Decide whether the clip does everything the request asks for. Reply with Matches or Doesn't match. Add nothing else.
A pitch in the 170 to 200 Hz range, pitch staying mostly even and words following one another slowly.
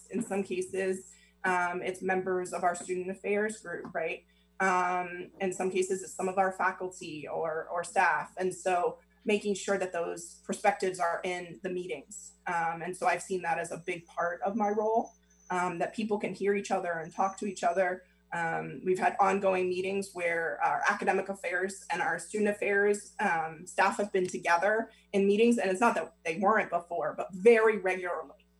Doesn't match